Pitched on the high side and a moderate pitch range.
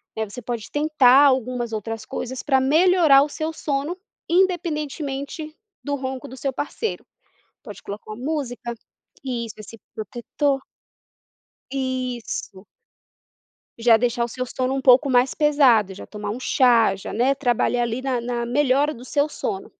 Yes: very high, 260 Hz; average, 3.4 semitones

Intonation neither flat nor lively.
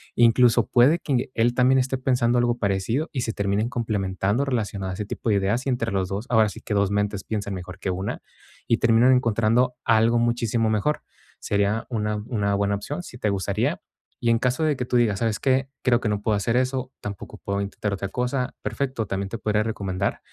Yes: average, 3.5 semitones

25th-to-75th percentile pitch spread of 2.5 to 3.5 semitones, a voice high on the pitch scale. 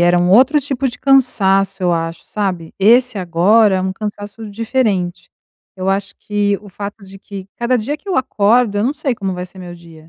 No: average, 4.2 semitones; high, 200 Hz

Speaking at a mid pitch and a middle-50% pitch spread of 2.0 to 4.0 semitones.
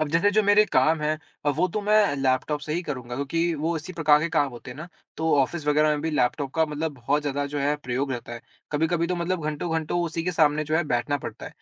Yes: medium, 155 Hz; average, 2.7 semitones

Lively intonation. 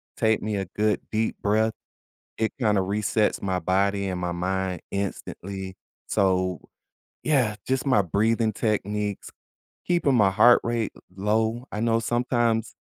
No: average, 2.8 semitones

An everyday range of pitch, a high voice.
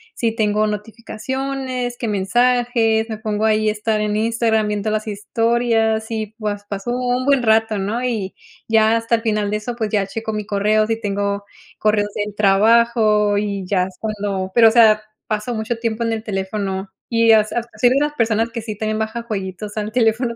No: narrow, 1.7 semitones; high, 220 Hz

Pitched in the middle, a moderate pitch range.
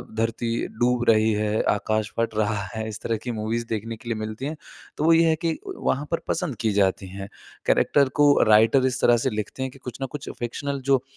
No: low, 115 Hz; average, 3.6 semitones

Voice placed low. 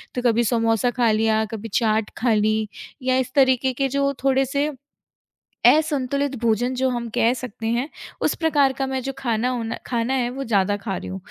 No: high, 245 Hz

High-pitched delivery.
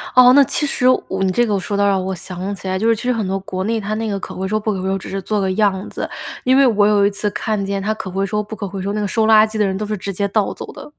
Yes: high, 205 Hz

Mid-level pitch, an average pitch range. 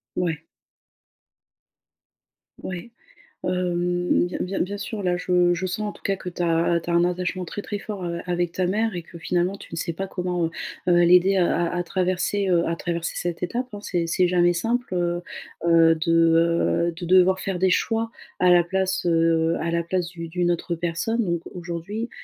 No: medium, 175 Hz; narrow, 1.6 semitones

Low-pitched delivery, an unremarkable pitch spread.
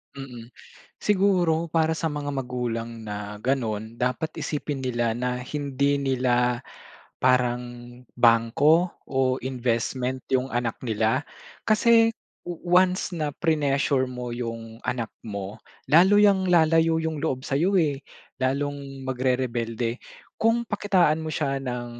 Yes: low, 130 Hz; average, 4.6 semitones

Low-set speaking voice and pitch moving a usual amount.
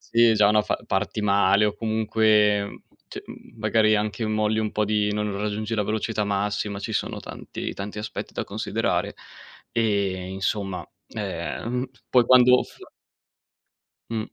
No: low, 105 Hz; narrow, 1.4 semitones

